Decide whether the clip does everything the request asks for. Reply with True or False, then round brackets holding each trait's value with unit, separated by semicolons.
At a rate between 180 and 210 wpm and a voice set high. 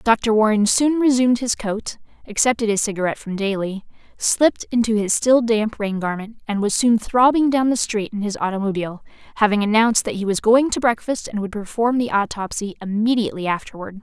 True (185 wpm; 220 Hz)